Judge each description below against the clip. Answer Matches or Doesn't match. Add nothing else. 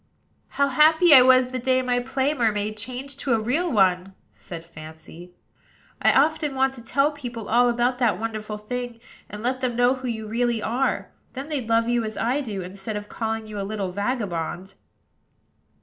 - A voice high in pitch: Matches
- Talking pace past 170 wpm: Matches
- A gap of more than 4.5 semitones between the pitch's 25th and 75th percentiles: Doesn't match